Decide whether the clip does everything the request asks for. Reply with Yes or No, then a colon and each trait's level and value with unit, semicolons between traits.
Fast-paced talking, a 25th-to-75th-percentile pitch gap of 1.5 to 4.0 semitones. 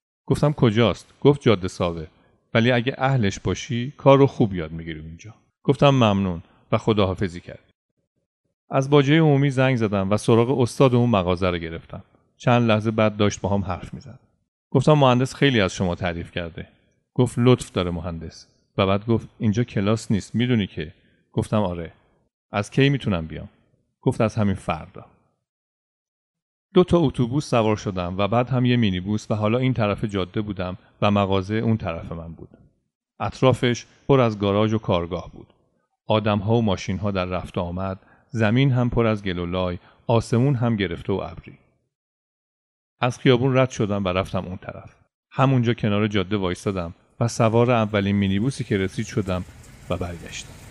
No: fast, 165 wpm; average, 4.7 semitones